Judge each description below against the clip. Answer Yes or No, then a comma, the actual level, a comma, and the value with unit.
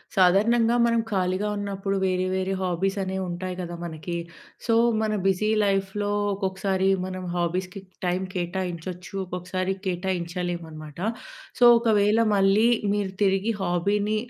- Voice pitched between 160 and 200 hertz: Yes, high, 190 Hz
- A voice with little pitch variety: Yes, narrow, 2.0 semitones